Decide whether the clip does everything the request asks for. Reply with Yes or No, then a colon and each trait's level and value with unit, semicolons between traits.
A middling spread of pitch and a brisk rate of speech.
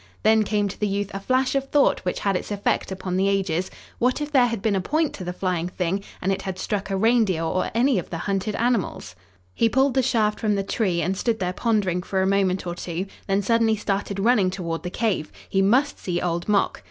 Yes: average, 3.6 semitones; fast, 240 wpm